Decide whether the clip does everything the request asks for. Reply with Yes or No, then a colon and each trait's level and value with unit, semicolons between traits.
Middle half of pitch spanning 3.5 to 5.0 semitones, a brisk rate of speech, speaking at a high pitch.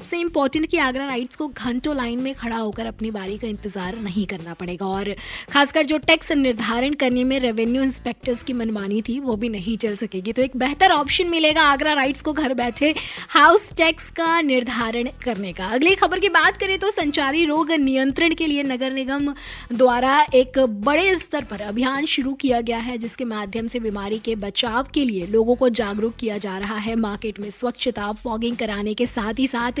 Yes: average, 4.2 semitones; fast, 195 wpm; very high, 250 Hz